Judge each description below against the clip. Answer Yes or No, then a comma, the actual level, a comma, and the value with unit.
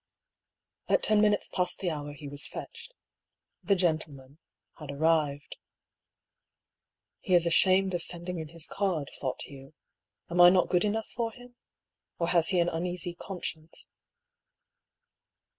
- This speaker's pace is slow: No, average, 150 wpm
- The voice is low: No, medium, 175 Hz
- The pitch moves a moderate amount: Yes, average, 3.7 semitones